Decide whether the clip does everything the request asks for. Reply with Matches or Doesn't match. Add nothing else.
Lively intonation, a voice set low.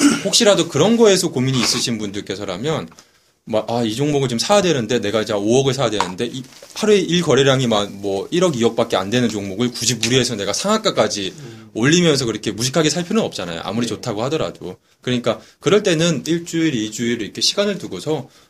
Matches